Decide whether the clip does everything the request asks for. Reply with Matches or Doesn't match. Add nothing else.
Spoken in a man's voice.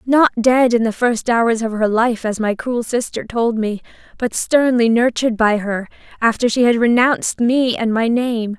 Doesn't match